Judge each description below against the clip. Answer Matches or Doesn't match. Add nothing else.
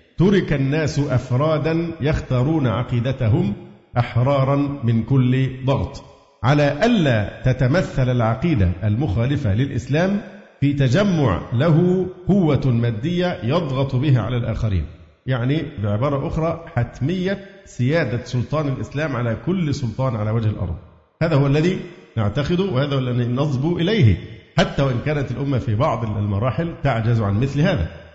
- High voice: Doesn't match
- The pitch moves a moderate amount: Matches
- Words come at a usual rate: Matches